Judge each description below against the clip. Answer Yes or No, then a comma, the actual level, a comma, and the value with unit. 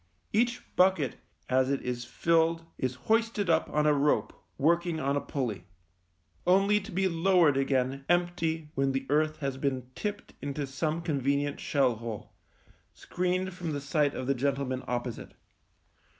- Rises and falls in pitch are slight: No, average, 4.5 semitones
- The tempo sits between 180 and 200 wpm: No, average, 155 wpm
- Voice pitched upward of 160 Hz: No, medium, 145 Hz